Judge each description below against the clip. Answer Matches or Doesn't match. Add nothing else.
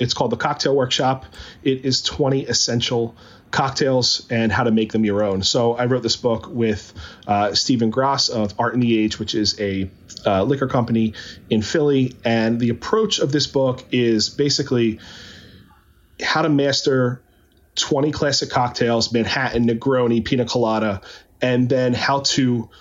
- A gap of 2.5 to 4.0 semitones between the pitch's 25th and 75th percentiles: Matches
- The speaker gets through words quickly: Doesn't match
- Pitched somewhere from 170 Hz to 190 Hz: Doesn't match